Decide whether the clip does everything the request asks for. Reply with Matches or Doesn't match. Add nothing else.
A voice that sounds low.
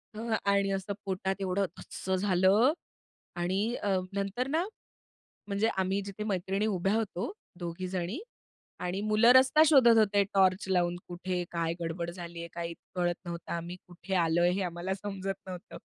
Doesn't match